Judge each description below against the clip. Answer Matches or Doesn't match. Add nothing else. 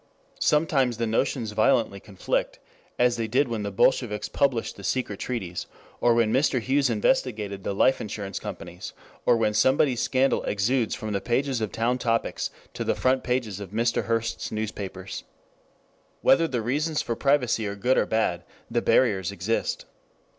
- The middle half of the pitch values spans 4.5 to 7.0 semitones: Doesn't match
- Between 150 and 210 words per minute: Matches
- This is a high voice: Doesn't match